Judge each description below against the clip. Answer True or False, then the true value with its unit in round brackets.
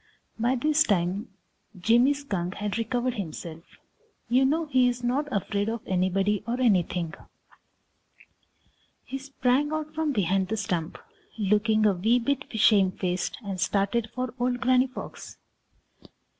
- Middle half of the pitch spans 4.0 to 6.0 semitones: True (4.7 semitones)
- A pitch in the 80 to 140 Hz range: False (225 Hz)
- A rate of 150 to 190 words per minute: False (135 wpm)